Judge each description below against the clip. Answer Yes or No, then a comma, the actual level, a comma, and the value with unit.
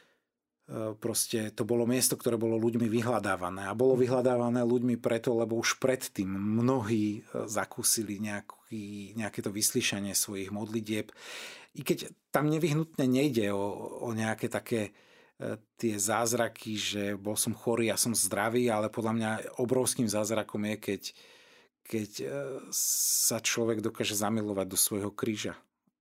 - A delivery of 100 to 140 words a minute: Yes, average, 130 wpm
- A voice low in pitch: Yes, low, 115 Hz